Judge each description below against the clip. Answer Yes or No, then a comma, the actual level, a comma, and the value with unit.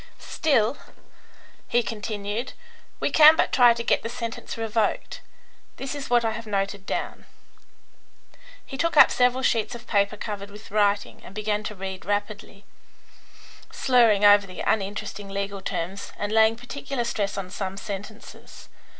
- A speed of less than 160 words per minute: Yes, average, 150 wpm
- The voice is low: No, high, 215 Hz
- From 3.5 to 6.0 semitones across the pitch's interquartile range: No, average, 2.8 semitones